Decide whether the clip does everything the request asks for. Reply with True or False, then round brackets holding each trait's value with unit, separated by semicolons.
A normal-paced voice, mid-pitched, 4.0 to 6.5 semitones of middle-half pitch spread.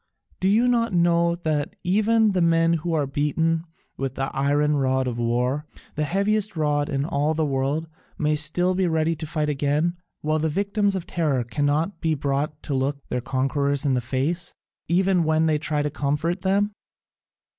False (180 wpm; 155 Hz; 3.5 semitones)